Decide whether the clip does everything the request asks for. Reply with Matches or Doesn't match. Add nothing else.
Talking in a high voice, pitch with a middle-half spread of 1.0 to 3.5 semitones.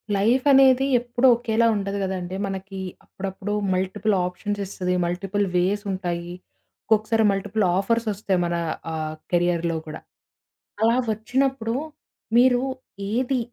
Doesn't match